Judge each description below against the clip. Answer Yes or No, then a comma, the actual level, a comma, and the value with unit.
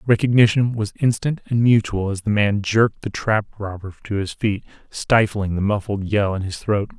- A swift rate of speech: No, average, 190 wpm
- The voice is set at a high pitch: No, low, 105 Hz